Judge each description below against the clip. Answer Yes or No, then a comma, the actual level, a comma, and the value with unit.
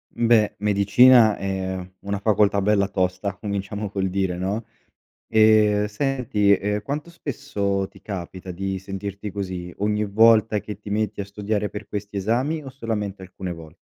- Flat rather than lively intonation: Yes, narrow, 1.8 semitones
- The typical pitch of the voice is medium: No, low, 100 Hz